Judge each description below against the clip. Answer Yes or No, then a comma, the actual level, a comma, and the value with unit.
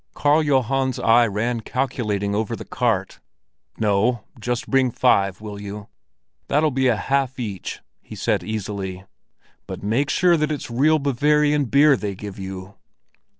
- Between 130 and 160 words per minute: Yes, average, 150 wpm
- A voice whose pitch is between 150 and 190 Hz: No, low, 120 Hz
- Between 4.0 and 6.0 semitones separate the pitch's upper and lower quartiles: Yes, average, 5.1 semitones